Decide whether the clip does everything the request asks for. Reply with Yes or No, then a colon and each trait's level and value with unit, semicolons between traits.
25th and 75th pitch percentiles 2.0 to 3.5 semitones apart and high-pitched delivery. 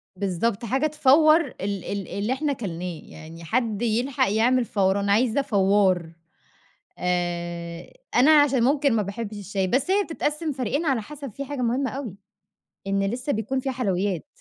No: wide, 5.5 semitones; high, 225 Hz